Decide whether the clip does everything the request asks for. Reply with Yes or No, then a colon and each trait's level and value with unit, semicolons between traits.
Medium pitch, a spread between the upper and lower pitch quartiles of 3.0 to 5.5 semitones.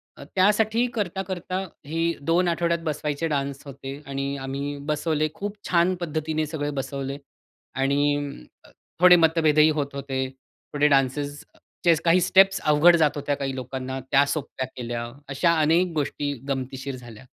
Yes: medium, 150 Hz; average, 3.5 semitones